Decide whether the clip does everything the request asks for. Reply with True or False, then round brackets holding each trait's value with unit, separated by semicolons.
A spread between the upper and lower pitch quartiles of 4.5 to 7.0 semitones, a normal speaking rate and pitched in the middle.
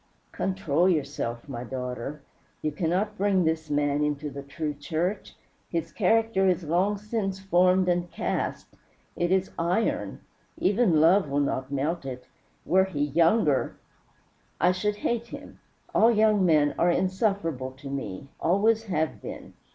True (5.0 semitones; 145 wpm; 170 Hz)